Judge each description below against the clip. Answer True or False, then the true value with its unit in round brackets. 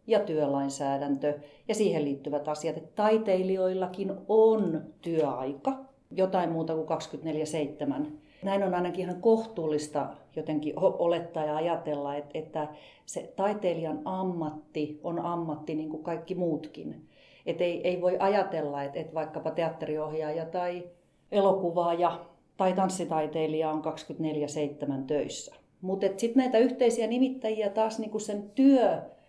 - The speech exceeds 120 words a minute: False (115 wpm)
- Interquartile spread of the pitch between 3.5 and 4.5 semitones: True (3.9 semitones)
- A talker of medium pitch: True (170 Hz)